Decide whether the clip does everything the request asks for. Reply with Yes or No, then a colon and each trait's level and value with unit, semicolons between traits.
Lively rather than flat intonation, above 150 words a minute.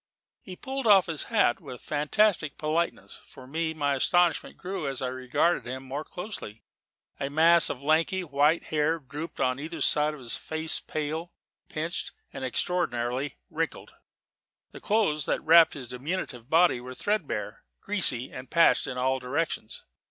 No: average, 4.5 semitones; average, 160 wpm